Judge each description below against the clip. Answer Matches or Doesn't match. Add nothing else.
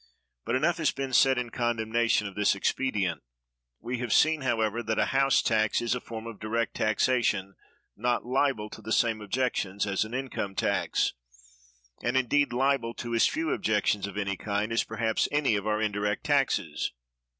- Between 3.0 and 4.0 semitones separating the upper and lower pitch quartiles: Matches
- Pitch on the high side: Doesn't match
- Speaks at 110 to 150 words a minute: Doesn't match